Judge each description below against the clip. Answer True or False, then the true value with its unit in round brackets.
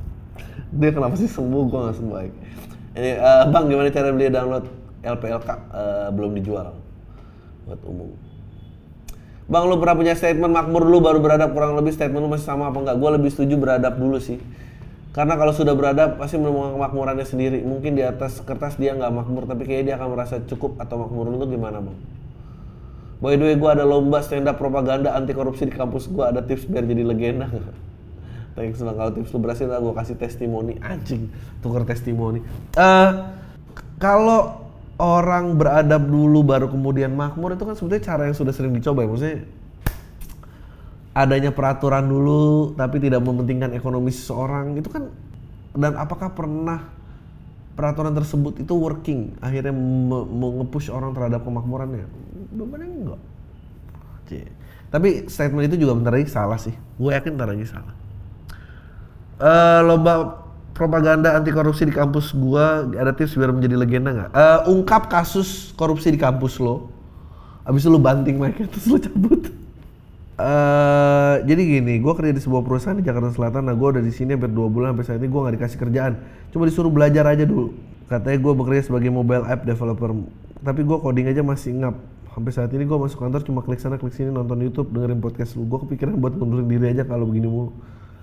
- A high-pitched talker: False (130 Hz)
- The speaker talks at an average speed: False (175 wpm)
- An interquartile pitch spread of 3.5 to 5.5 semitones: True (3.8 semitones)